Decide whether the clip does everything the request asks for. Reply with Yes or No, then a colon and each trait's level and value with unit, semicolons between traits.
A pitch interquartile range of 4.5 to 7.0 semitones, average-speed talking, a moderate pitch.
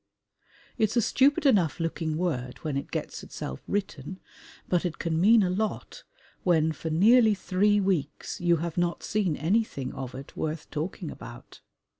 Yes: average, 4.8 semitones; average, 160 wpm; medium, 175 Hz